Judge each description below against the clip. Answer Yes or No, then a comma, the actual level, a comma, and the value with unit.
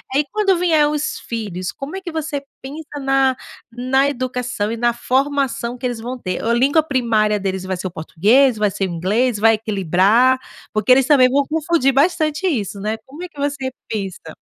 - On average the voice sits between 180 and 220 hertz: No, very high, 255 Hz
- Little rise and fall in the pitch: No, average, 5.1 semitones